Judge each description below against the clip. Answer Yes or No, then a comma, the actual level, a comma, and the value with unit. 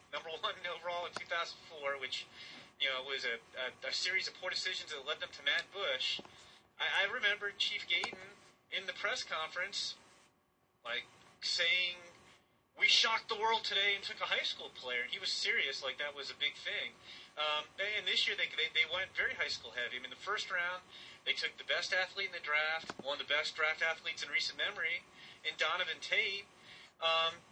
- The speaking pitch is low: No, medium, 175 Hz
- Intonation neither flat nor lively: Yes, average, 4.7 semitones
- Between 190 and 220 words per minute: Yes, average, 200 wpm